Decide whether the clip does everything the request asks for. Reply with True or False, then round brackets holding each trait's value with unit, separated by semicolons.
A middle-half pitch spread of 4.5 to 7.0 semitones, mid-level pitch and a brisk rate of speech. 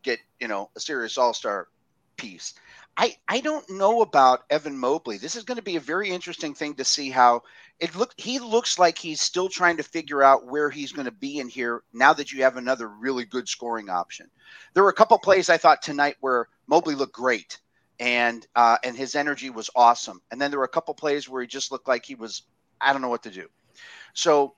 True (4.8 semitones; 145 Hz; 225 wpm)